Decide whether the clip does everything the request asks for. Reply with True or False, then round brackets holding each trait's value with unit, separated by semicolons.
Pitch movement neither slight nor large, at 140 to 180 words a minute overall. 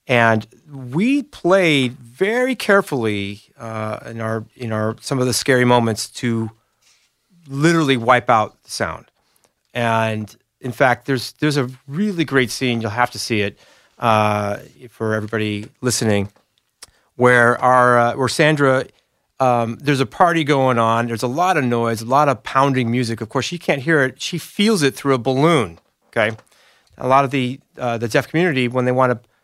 True (3.7 semitones; 175 wpm)